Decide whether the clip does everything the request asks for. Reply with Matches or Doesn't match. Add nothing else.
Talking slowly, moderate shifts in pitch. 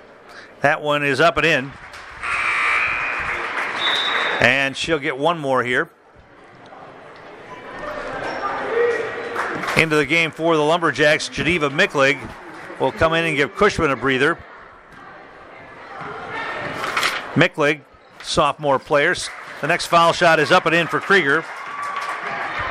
Matches